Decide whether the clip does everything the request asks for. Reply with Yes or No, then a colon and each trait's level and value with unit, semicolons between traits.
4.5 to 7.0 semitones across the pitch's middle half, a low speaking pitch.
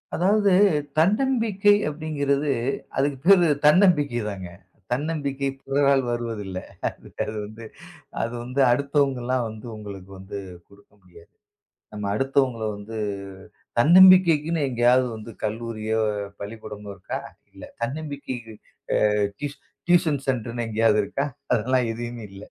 Yes: average, 5.2 semitones; low, 130 Hz